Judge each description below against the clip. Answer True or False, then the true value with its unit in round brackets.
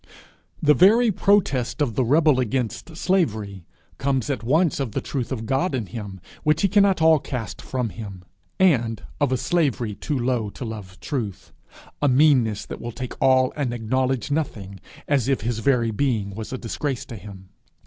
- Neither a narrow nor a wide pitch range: True (4.7 semitones)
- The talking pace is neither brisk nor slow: True (180 wpm)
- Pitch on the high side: False (130 Hz)